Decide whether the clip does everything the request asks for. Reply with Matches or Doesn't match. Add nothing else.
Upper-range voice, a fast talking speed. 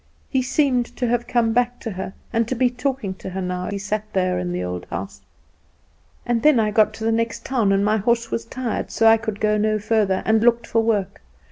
Matches